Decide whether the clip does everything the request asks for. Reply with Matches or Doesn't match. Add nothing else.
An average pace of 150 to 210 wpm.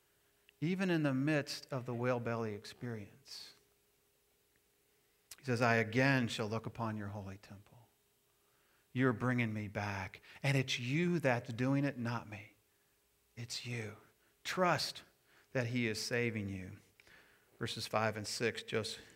Doesn't match